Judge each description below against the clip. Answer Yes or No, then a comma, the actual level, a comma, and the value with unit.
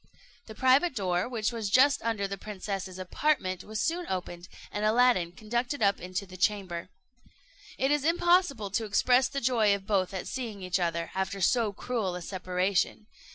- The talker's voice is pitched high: Yes, high, 205 Hz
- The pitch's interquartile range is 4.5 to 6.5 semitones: Yes, average, 5.0 semitones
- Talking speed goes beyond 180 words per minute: No, average, 170 wpm